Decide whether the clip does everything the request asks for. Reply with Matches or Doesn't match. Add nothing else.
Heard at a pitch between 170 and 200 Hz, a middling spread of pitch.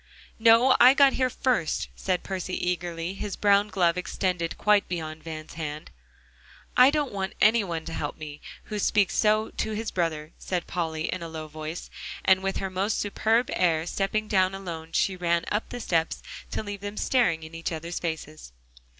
Matches